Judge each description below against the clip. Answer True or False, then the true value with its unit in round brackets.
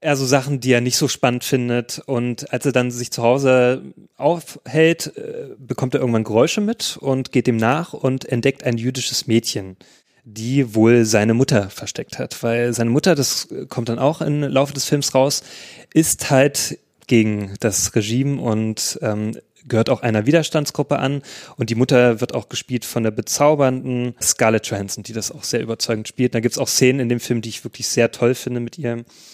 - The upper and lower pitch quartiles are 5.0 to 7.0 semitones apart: False (3.1 semitones)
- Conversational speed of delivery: False (195 wpm)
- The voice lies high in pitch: False (125 Hz)